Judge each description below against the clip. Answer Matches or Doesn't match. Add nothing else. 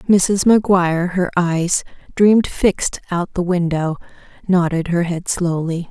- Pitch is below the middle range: Doesn't match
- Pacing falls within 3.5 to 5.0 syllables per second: Matches